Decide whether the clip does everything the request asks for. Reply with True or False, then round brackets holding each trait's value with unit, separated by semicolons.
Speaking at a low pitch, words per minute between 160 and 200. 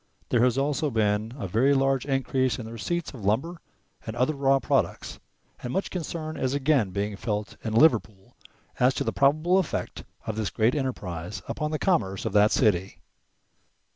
True (125 Hz; 175 wpm)